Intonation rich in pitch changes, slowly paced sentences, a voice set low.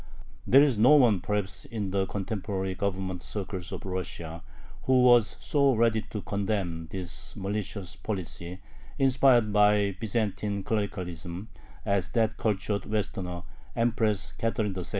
No: average, 3.0 semitones; slow, 130 wpm; low, 100 Hz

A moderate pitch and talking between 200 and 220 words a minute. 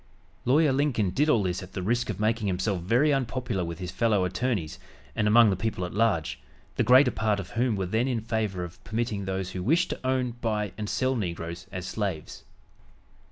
No: low, 105 Hz; fast, 205 wpm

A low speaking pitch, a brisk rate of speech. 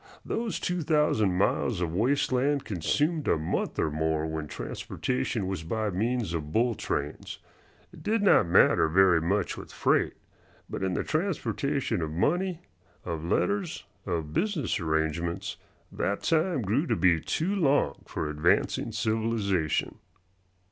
No: low, 105 Hz; average, 140 wpm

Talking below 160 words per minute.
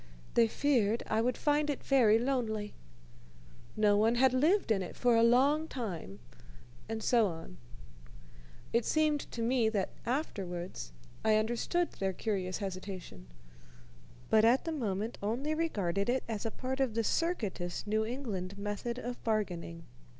Yes: average, 150 wpm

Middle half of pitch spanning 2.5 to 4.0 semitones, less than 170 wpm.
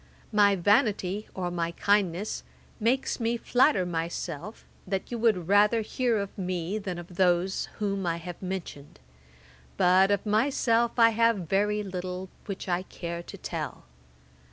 Yes: average, 3.3 semitones; average, 150 wpm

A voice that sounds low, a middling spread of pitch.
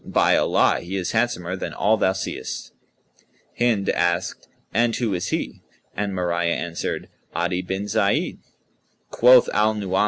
Yes: very low, 95 Hz; average, 3.5 semitones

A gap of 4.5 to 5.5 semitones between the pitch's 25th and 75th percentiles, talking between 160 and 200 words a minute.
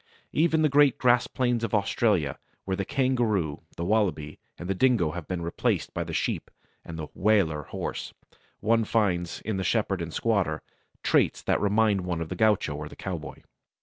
Yes: average, 5.2 semitones; average, 180 wpm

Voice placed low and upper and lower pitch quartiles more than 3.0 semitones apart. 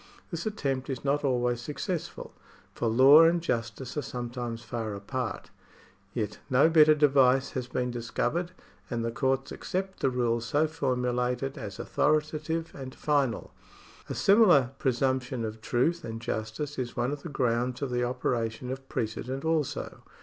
Yes: low, 130 Hz; average, 3.5 semitones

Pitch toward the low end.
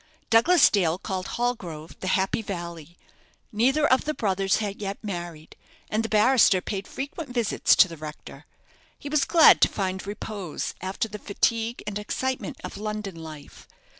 No: high, 205 Hz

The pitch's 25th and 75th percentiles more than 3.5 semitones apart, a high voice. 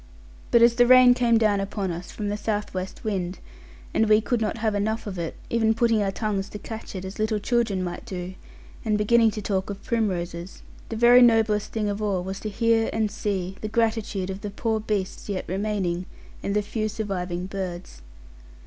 No: average, 2.7 semitones; high, 210 Hz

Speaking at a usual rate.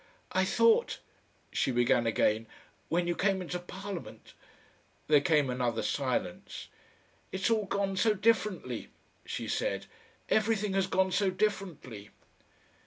No: slow, 125 wpm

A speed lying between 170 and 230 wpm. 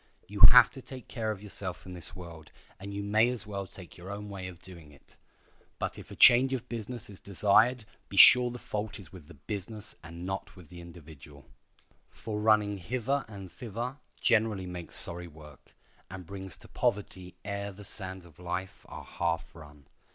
Yes: average, 190 wpm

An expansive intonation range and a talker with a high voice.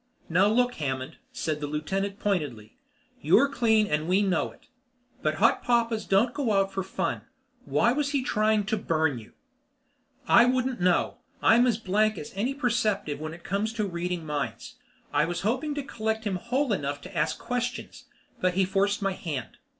Yes: wide, 5.9 semitones; high, 200 Hz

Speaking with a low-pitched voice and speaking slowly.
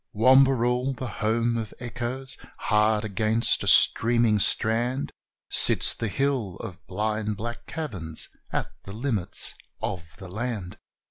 Yes: low, 115 Hz; slow, 125 wpm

